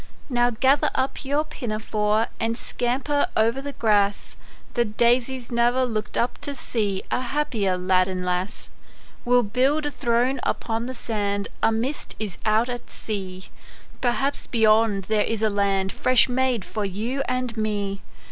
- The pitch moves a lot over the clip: No, average, 3.4 semitones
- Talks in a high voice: Yes, high, 230 Hz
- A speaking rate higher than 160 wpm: No, average, 155 wpm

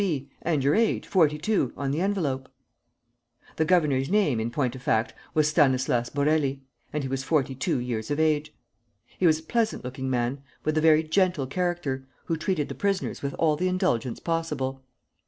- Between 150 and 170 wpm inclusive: No, average, 185 wpm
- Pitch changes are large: No, average, 3.9 semitones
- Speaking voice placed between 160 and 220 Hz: No, medium, 150 Hz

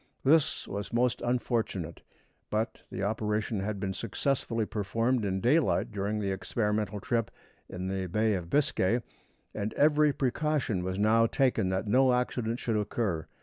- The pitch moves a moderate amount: Yes, average, 3.9 semitones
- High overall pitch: No, low, 110 Hz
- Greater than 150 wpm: No, average, 145 wpm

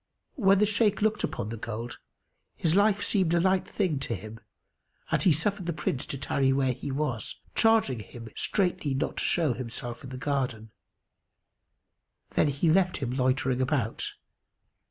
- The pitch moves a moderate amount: No, wide, 6.9 semitones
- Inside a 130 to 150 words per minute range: No, average, 165 wpm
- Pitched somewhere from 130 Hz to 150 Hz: Yes, medium, 140 Hz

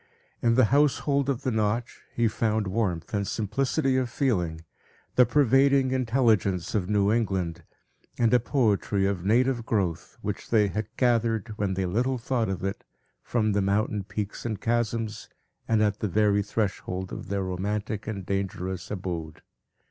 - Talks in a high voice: No, low, 105 Hz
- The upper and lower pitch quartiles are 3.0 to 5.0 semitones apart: Yes, average, 3.4 semitones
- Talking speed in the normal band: Yes, average, 155 wpm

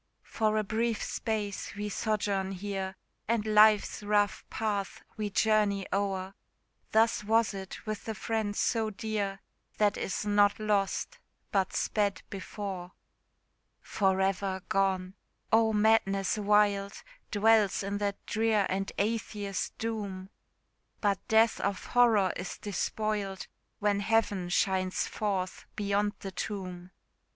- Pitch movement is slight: Yes, narrow, 1.7 semitones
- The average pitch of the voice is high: Yes, high, 205 Hz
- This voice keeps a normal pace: No, slow, 120 wpm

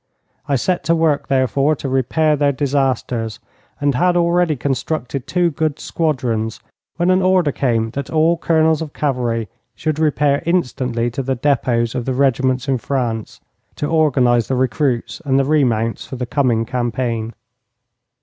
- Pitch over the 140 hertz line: No, low, 135 Hz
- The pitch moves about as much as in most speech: Yes, average, 4.1 semitones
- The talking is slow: No, average, 155 wpm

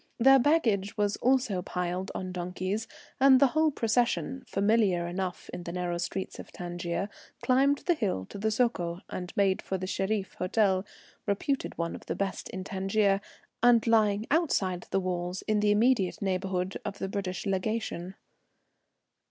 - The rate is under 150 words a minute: No, average, 160 wpm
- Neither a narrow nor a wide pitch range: Yes, average, 3.7 semitones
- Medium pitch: No, high, 195 Hz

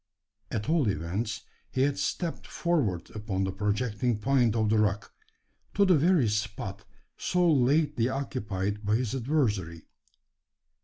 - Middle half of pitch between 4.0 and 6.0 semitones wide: Yes, average, 5.1 semitones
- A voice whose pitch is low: Yes, low, 110 Hz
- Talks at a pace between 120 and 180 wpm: Yes, slow, 135 wpm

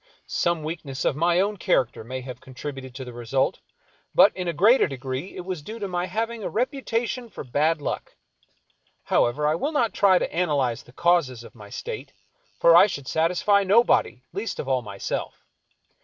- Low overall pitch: No, medium, 165 Hz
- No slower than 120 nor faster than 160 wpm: No, average, 185 wpm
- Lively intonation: Yes, wide, 7.4 semitones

